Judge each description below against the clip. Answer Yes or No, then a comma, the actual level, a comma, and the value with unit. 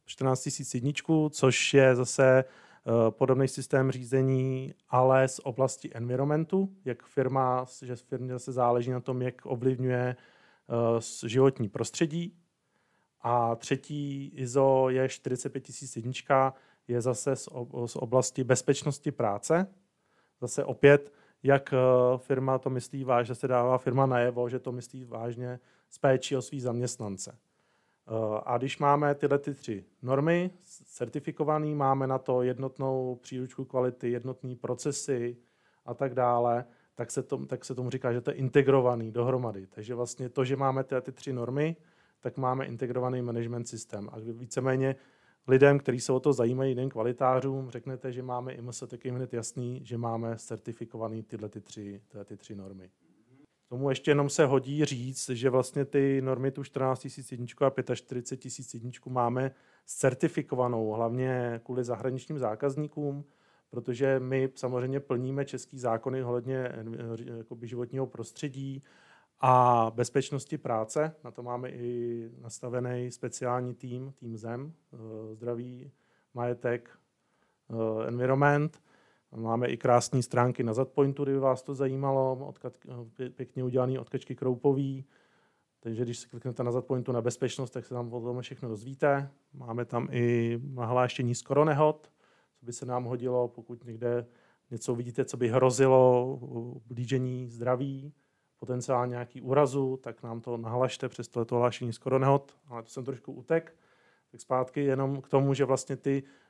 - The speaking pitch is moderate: No, low, 130 Hz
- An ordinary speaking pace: Yes, average, 140 wpm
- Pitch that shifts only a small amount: Yes, narrow, 1.9 semitones